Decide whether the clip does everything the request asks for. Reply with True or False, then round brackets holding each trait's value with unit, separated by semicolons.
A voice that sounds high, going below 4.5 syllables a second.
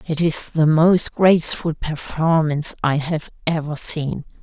False (160 Hz; 4.1 syllables/s)